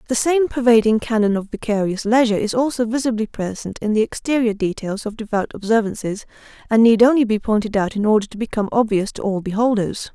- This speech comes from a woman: Yes, female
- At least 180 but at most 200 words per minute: Yes, average, 190 wpm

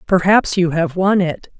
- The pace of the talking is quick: No, average, 190 wpm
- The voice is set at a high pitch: No, medium, 180 Hz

